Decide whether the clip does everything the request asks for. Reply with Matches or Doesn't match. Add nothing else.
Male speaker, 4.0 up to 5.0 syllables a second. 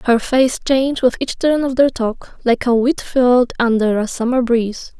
Doesn't match